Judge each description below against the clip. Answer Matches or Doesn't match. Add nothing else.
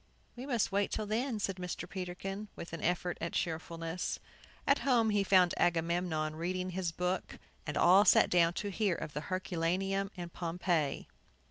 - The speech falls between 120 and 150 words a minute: Doesn't match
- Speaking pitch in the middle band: Matches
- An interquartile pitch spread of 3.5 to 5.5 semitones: Doesn't match